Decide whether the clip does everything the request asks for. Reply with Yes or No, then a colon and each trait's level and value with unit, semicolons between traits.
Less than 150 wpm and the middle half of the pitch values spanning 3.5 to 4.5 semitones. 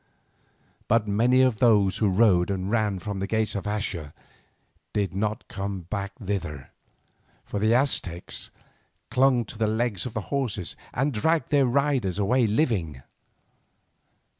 Yes: average, 140 wpm; average, 3.8 semitones